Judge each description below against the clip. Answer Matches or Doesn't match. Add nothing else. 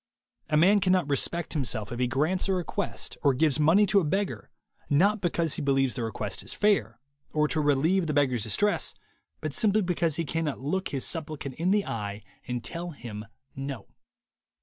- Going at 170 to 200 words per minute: Matches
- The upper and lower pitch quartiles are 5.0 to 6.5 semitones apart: Matches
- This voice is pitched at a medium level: Matches